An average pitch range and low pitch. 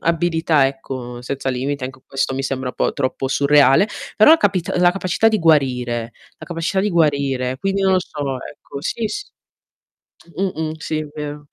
No: average, 4.9 semitones; medium, 145 Hz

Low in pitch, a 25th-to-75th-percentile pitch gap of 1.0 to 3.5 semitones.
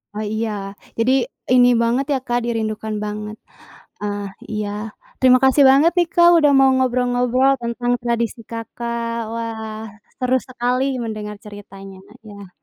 No: high, 235 Hz; average, 2.8 semitones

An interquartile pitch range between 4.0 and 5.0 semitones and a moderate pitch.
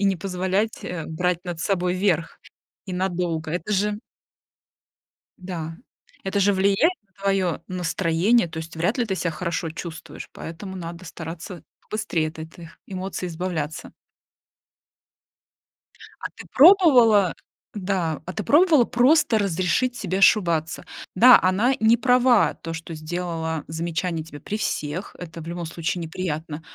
No: average, 3.5 semitones; medium, 180 Hz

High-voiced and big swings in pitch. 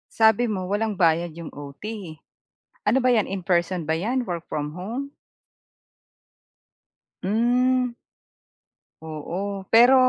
Yes: high, 200 Hz; wide, 5.9 semitones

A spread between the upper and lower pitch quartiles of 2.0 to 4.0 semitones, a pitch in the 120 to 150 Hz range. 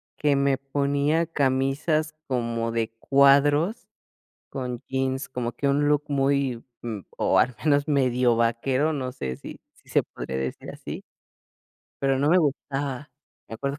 Yes: narrow, 2.4 semitones; low, 135 Hz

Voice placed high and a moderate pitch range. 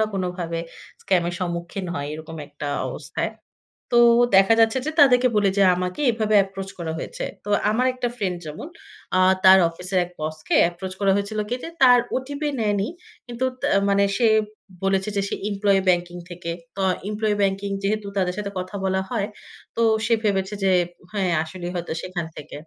Yes: high, 195 Hz; average, 3.1 semitones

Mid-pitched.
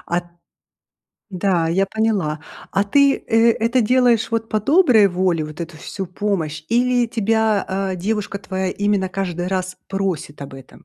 No: high, 195 Hz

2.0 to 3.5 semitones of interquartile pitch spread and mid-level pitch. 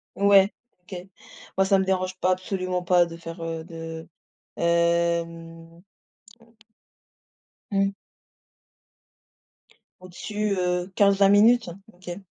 Yes: narrow, 2.4 semitones; medium, 180 Hz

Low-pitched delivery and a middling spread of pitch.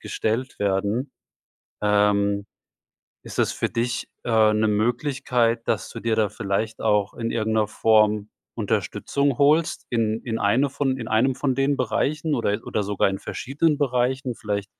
Yes: low, 115 Hz; average, 3.7 semitones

